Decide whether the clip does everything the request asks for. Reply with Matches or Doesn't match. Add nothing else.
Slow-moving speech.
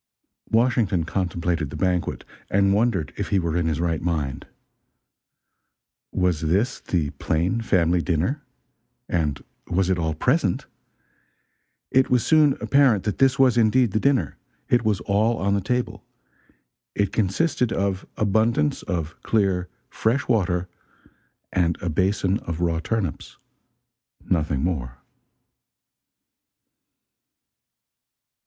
Matches